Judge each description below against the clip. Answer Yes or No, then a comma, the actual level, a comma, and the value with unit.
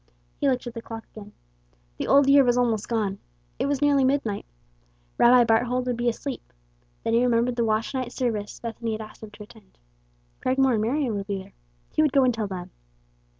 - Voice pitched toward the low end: No, high, 235 Hz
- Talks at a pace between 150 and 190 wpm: No, fast, 205 wpm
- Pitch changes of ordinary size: Yes, average, 3.0 semitones